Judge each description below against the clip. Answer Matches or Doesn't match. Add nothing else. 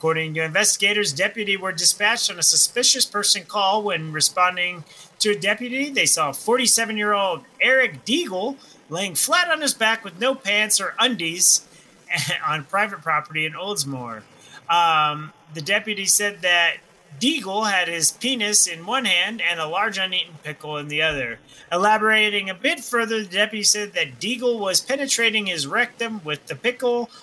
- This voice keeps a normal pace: Matches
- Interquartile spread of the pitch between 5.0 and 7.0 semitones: Matches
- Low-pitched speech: Doesn't match